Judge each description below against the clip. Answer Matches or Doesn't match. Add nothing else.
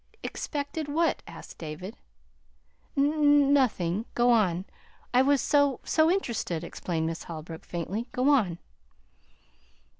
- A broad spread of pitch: Matches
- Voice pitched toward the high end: Matches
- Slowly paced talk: Matches